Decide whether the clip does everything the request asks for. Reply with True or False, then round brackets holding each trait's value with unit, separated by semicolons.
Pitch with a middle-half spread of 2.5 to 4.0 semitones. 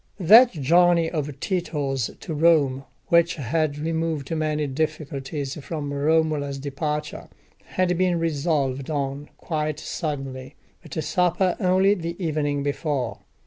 True (2.9 semitones)